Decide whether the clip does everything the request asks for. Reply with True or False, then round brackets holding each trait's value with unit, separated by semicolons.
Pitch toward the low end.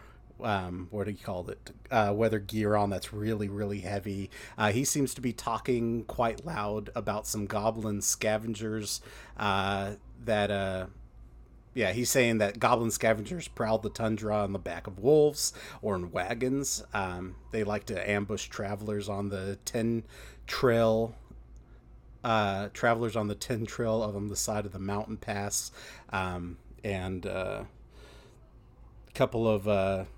True (105 Hz)